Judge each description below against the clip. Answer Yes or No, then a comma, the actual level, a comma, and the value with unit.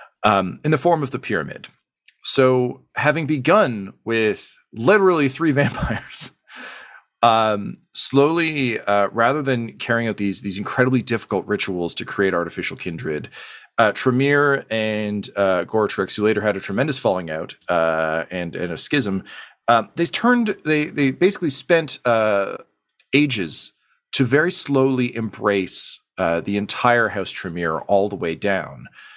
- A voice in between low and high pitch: No, low, 120 Hz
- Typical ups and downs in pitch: No, wide, 5.9 semitones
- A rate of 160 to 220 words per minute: No, average, 140 wpm